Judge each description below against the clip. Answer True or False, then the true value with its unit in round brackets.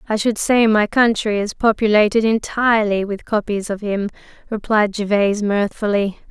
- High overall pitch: True (210 Hz)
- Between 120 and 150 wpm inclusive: True (145 wpm)